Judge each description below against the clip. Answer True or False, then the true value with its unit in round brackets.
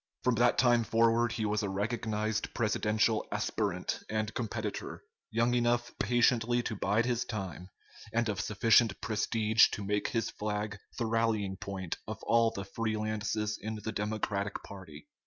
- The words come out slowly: False (155 wpm)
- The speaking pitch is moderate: False (110 Hz)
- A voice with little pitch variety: True (1.9 semitones)